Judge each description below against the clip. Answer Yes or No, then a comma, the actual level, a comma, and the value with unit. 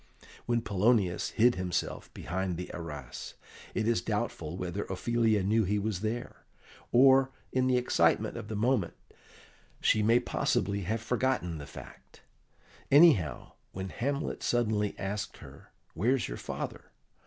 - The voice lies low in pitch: Yes, low, 105 Hz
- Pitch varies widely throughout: No, average, 4.7 semitones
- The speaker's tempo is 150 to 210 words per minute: No, slow, 135 wpm